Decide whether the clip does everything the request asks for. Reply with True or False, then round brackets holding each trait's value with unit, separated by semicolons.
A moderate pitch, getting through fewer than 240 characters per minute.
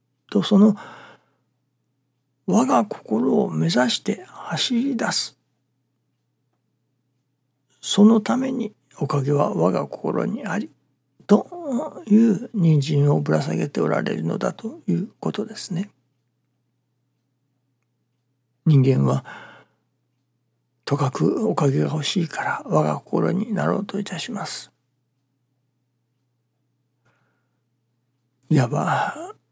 False (130 Hz; 175 characters per minute)